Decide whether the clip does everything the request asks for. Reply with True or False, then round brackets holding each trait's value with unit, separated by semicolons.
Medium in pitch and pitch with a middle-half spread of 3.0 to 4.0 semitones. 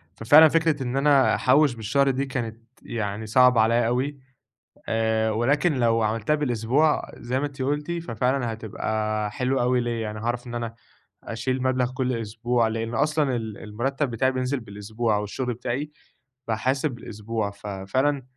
False (120 Hz; 3.3 semitones)